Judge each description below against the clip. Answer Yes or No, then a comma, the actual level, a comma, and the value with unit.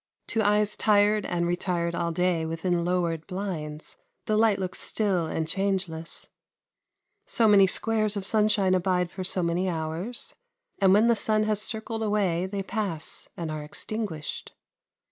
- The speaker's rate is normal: Yes, average, 150 wpm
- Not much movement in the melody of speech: No, average, 3.7 semitones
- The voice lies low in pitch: No, high, 190 Hz